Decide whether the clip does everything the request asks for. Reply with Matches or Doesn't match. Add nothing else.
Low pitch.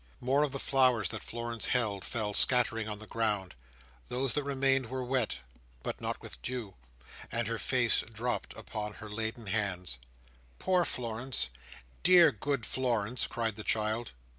Matches